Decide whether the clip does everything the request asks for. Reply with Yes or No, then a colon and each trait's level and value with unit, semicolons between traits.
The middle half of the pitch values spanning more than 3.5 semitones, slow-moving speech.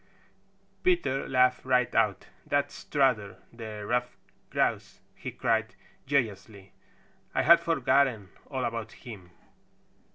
Yes: average, 4.1 semitones; slow, 105 wpm